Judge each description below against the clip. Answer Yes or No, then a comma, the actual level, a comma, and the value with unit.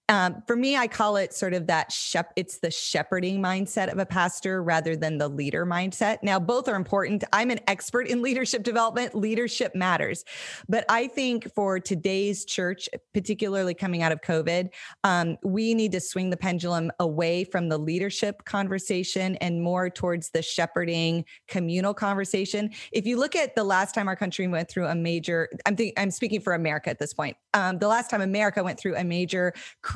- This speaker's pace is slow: No, average, 190 wpm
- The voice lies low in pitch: No, high, 190 Hz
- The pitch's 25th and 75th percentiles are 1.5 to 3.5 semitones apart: Yes, average, 3.2 semitones